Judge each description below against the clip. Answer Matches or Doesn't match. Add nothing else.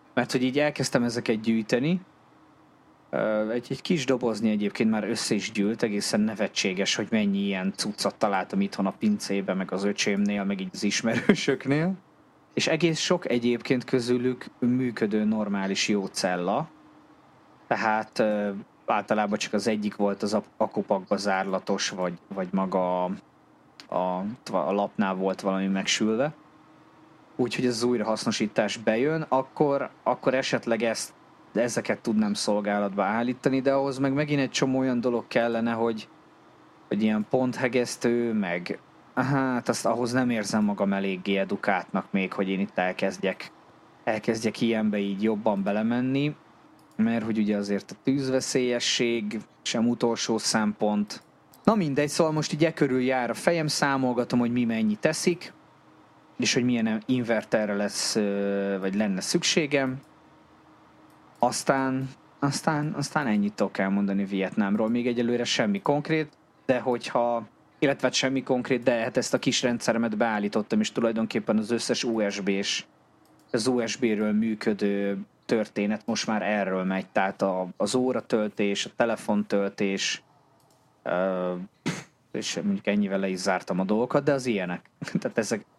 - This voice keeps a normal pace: Matches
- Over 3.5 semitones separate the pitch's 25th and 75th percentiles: Matches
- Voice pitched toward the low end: Matches